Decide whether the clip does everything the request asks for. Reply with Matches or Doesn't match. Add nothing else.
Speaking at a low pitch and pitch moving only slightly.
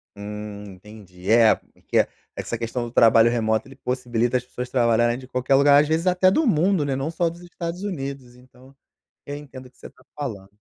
Doesn't match